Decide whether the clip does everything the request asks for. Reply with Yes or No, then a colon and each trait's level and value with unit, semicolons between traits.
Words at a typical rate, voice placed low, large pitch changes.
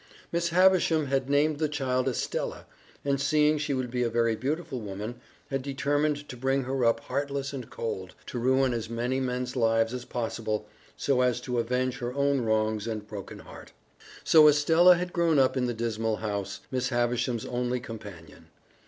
No: average, 180 wpm; low, 125 Hz; average, 3.4 semitones